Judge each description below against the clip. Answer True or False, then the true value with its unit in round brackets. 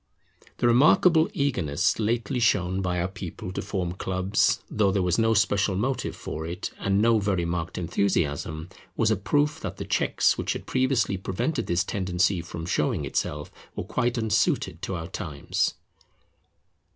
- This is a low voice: True (95 Hz)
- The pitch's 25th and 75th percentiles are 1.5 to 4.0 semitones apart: False (4.6 semitones)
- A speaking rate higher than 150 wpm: True (160 wpm)